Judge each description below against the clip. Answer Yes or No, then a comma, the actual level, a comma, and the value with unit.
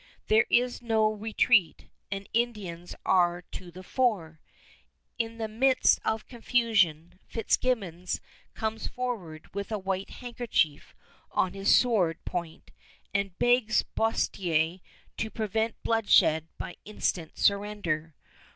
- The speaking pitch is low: No, high, 205 Hz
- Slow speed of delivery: Yes, slow, 115 wpm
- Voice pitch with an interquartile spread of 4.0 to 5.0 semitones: Yes, average, 4.4 semitones